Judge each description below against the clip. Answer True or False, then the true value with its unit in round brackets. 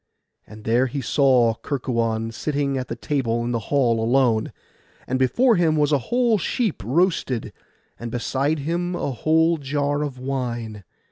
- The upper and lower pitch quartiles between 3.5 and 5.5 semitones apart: True (4.4 semitones)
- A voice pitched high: False (135 Hz)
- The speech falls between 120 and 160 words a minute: True (155 wpm)